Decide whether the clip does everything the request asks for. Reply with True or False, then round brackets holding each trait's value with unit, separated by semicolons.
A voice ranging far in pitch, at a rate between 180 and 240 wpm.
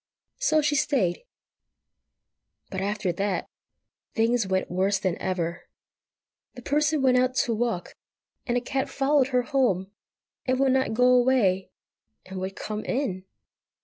False (5.7 semitones; 140 wpm)